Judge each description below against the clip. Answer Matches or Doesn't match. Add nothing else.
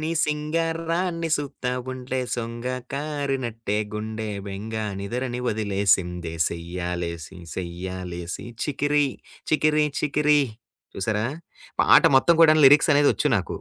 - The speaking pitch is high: Doesn't match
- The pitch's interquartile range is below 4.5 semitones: Doesn't match